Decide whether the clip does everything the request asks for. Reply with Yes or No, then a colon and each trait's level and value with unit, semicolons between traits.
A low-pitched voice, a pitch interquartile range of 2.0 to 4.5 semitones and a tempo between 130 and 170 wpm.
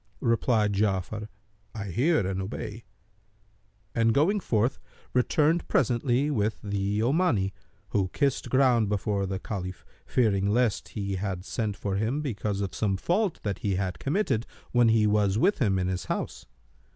Yes: low, 105 Hz; average, 4.2 semitones; average, 150 wpm